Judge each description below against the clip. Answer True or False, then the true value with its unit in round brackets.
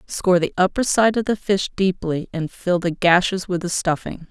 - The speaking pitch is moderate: True (180 Hz)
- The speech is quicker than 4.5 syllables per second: True (5.0 syllables/s)